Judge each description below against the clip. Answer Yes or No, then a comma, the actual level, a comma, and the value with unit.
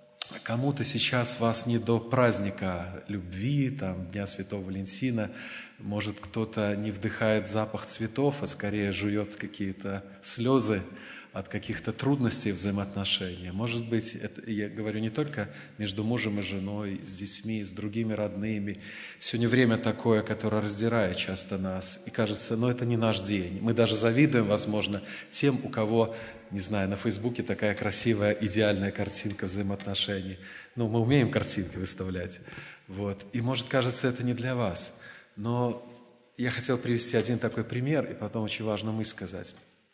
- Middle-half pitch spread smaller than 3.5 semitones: Yes, average, 2.7 semitones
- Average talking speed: Yes, average, 145 wpm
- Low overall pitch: Yes, low, 110 Hz